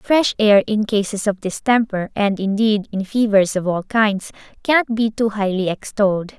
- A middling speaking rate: Yes, average, 170 wpm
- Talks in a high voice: Yes, high, 210 Hz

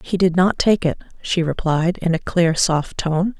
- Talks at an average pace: No, fast, 210 wpm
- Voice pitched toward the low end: No, medium, 170 Hz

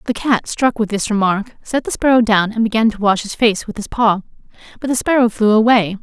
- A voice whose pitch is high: Yes, high, 220 Hz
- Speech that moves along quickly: Yes, fast, 240 wpm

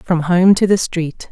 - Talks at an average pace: No, fast, 230 wpm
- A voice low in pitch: No, medium, 175 Hz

